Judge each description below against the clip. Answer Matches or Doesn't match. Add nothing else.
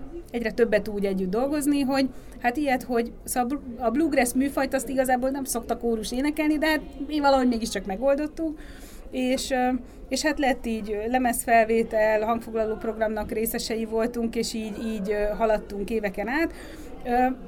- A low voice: Doesn't match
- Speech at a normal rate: Matches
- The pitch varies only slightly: Doesn't match